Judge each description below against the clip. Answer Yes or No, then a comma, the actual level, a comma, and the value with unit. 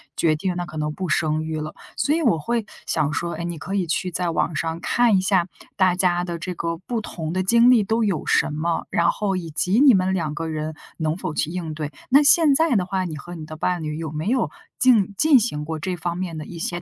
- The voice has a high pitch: No, medium, 175 Hz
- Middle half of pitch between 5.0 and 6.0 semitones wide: No, average, 3.8 semitones